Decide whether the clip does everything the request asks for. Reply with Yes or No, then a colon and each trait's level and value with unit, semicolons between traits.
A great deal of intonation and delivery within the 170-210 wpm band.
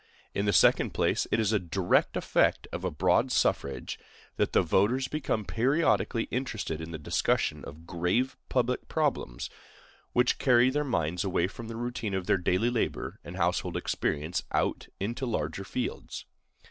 No: wide, 5.8 semitones; average, 160 wpm